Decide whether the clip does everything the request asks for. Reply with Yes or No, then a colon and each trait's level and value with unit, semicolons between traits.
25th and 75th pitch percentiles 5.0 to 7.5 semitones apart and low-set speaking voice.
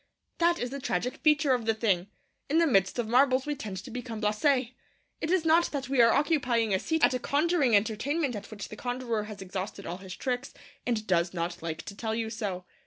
No: wide, 5.4 semitones; high, 235 Hz